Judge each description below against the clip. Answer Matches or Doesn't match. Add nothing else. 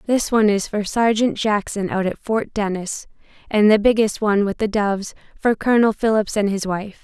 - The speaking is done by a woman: Matches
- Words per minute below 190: Doesn't match